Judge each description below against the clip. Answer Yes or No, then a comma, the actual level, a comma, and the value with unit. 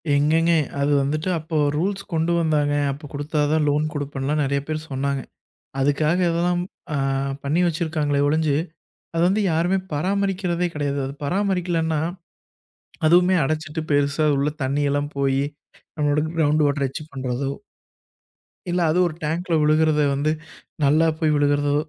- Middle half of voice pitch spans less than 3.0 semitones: Yes, narrow, 2.6 semitones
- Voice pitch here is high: No, medium, 155 Hz